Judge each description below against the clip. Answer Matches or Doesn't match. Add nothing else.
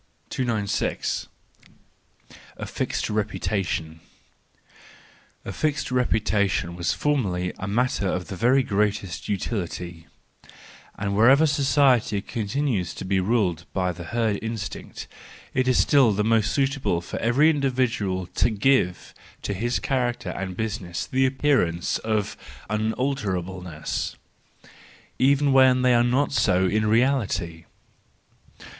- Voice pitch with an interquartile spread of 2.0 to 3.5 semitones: Doesn't match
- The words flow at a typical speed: Doesn't match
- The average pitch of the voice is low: Matches